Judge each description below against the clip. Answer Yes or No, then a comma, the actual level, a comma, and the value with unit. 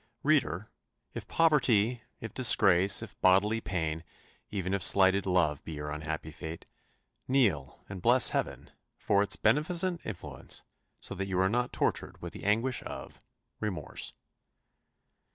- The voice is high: No, low, 100 Hz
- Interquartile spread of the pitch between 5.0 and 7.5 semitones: Yes, wide, 5.4 semitones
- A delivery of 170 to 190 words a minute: No, slow, 135 wpm